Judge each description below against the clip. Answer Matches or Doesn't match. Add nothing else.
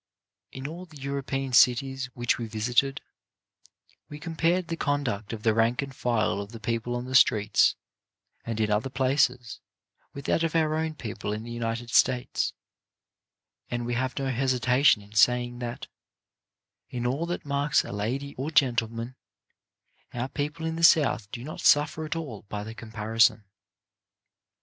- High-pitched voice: Doesn't match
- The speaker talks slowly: Doesn't match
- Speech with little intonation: Doesn't match